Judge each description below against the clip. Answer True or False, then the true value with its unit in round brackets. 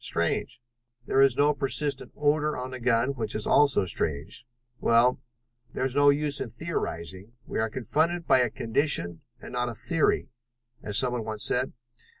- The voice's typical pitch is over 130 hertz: False (125 Hz)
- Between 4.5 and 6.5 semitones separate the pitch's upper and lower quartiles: False (4.1 semitones)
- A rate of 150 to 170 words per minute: True (160 wpm)